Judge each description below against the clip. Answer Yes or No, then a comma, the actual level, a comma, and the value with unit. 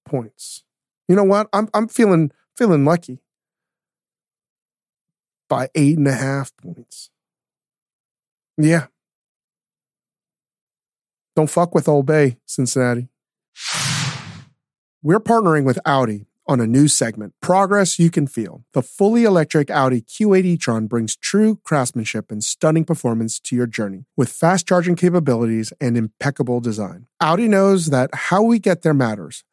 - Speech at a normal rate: No, slow, 130 wpm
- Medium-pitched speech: Yes, medium, 150 Hz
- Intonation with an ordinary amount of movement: No, wide, 6.3 semitones